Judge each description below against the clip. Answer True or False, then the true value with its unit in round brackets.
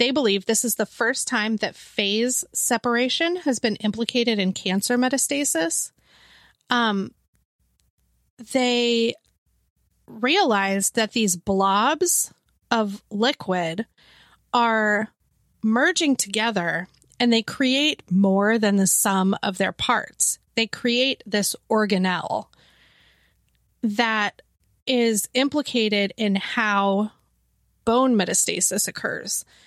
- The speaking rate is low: True (100 wpm)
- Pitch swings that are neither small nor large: True (3.5 semitones)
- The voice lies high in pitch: True (225 Hz)